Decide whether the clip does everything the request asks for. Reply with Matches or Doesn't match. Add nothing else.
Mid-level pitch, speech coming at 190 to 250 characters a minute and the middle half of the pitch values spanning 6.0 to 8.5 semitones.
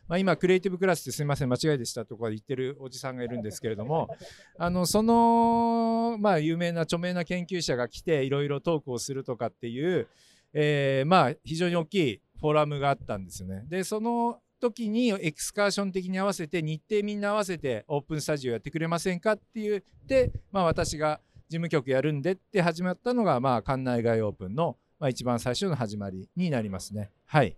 Doesn't match